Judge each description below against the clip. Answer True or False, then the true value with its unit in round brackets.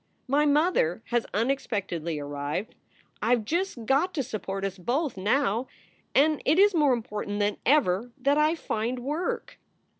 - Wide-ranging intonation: True (6.4 semitones)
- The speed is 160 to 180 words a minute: False (150 wpm)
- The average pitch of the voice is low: False (245 Hz)